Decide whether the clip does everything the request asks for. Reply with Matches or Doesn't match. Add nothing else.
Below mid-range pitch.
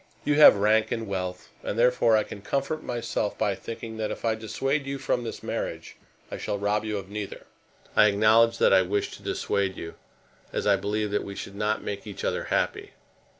Matches